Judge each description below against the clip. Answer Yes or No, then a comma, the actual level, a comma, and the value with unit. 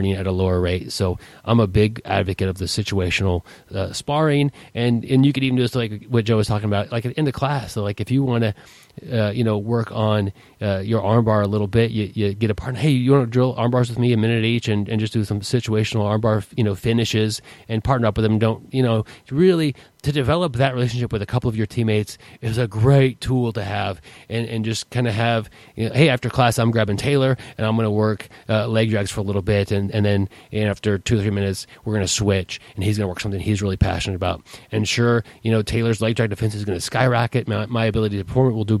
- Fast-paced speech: Yes, fast, 260 wpm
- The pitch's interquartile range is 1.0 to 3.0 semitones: Yes, average, 2.7 semitones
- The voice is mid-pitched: No, low, 110 Hz